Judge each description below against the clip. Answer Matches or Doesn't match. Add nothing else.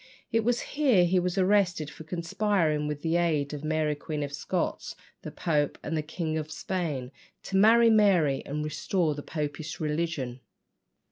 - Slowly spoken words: Doesn't match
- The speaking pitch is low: Doesn't match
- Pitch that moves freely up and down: Doesn't match